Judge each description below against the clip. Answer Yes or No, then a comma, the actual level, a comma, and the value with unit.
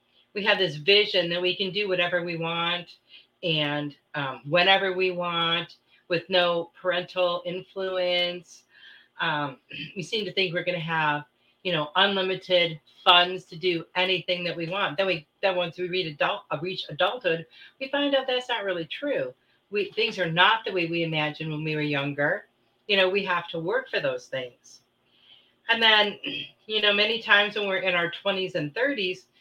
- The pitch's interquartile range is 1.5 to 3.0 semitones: Yes, average, 2.7 semitones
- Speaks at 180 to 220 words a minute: Yes, average, 185 wpm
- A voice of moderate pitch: Yes, medium, 180 Hz